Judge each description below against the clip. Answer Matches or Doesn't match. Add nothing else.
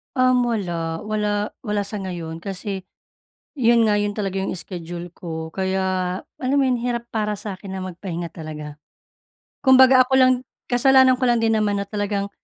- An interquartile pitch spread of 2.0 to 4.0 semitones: Doesn't match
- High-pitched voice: Matches